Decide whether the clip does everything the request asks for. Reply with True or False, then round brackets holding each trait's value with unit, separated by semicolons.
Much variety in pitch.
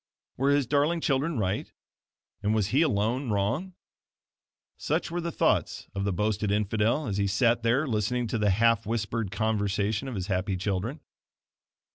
False (4.6 semitones)